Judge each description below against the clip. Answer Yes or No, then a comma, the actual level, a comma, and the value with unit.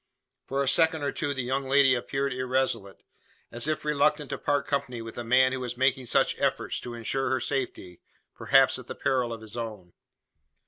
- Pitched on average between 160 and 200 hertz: No, low, 130 Hz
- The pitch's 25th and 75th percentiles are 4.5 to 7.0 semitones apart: No, narrow, 2.6 semitones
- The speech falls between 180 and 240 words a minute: Yes, average, 195 wpm